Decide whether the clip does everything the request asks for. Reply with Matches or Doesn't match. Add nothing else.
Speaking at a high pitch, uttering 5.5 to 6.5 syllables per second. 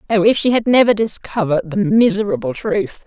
Matches